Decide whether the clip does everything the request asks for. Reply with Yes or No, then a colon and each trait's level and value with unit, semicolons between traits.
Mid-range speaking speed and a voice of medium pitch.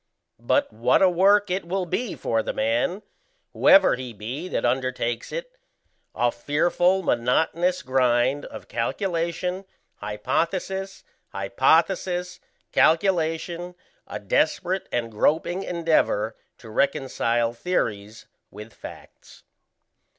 No: slow, 105 wpm; medium, 160 Hz